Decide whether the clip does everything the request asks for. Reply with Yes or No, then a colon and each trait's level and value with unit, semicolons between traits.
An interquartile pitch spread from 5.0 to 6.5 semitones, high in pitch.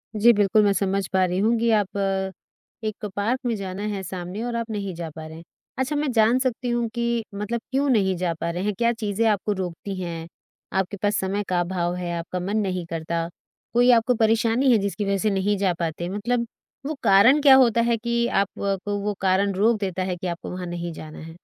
No: average, 4.1 semitones; high, 200 Hz